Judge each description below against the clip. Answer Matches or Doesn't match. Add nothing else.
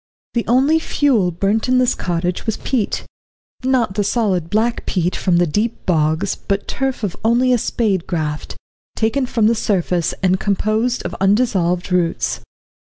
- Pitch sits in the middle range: Doesn't match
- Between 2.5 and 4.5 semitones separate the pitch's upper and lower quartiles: Doesn't match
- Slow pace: Doesn't match